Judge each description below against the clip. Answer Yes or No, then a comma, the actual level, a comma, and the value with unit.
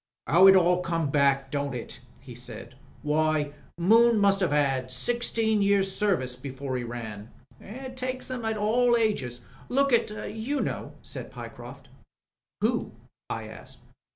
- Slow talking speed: No, average, 155 wpm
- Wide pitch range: Yes, wide, 8.5 semitones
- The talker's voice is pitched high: No, medium, 175 Hz